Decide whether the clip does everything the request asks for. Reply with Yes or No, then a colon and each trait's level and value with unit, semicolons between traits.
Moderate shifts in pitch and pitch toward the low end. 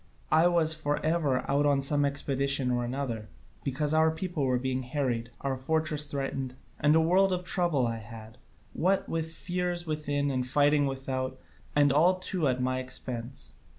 No: average, 3.6 semitones; medium, 145 Hz